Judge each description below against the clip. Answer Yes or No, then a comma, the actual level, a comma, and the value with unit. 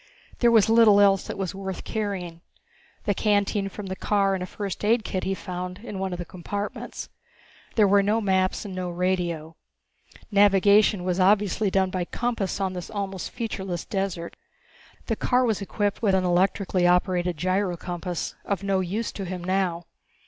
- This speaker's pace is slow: No, average, 170 wpm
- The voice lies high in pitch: Yes, high, 195 Hz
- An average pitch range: No, narrow, 2.1 semitones